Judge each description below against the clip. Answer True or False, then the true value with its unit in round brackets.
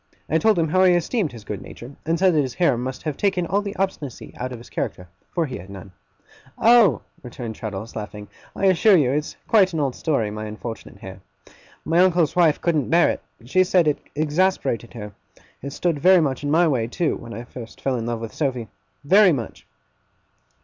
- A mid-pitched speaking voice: True (145 Hz)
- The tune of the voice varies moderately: False (7.0 semitones)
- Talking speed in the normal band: False (210 wpm)